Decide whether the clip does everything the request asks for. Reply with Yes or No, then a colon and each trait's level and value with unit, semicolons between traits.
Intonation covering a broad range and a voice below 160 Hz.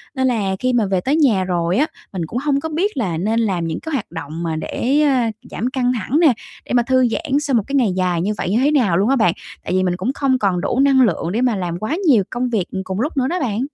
No: wide, 6.3 semitones; high, 230 Hz